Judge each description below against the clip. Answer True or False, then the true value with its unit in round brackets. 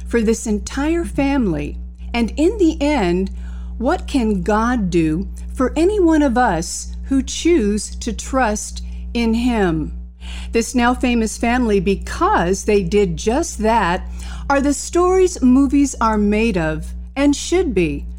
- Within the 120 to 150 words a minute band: True (140 wpm)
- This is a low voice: False (220 Hz)